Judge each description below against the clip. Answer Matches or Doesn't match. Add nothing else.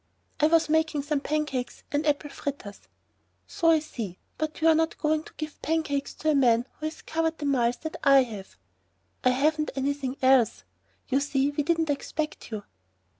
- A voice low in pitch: Doesn't match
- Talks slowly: Doesn't match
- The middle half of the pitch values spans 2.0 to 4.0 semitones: Matches